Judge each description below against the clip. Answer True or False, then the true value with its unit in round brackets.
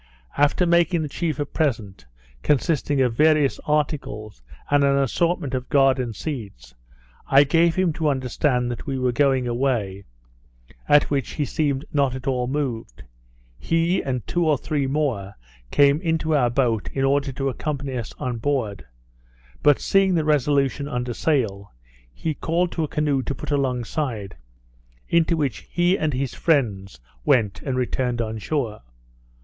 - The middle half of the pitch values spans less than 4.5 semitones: True (3.7 semitones)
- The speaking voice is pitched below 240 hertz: True (140 Hz)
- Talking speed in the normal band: True (155 wpm)